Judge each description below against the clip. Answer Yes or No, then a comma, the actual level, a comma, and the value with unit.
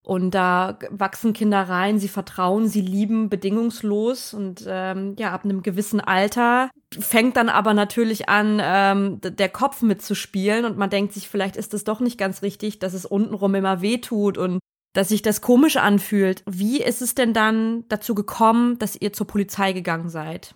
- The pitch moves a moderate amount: No, narrow, 2.3 semitones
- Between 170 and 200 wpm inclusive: Yes, average, 185 wpm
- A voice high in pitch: Yes, high, 205 Hz